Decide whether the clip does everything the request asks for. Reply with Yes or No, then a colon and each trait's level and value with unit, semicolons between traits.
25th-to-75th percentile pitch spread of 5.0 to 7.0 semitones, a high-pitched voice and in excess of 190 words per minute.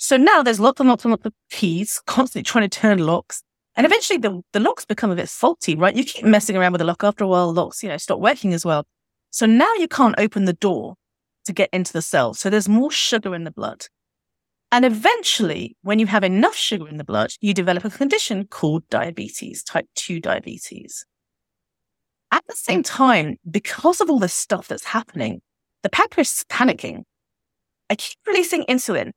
Yes: wide, 5.6 semitones; high, 210 Hz; fast, 205 wpm